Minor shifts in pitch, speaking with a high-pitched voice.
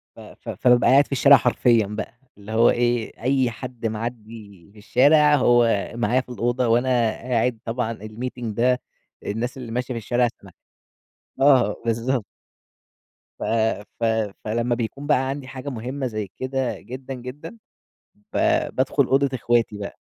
No: narrow, 2.2 semitones; low, 120 Hz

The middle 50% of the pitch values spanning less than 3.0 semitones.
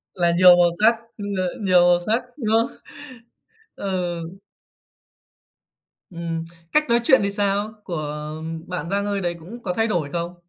No: average, 3.5 semitones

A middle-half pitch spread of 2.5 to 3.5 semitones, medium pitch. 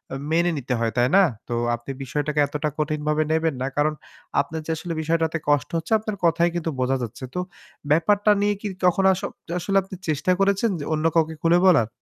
Yes: average, 3.1 semitones; medium, 160 Hz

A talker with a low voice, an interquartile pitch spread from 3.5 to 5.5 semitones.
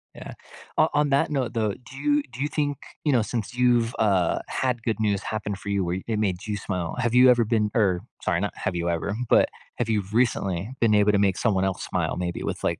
Yes: low, 110 Hz; average, 4.0 semitones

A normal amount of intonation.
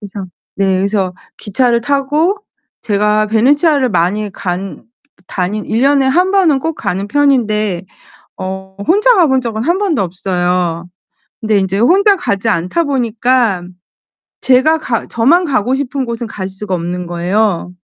No: wide, 6.4 semitones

